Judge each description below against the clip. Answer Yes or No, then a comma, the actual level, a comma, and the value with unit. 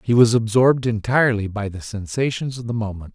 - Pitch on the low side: Yes, low, 115 Hz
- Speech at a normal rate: Yes, average, 190 wpm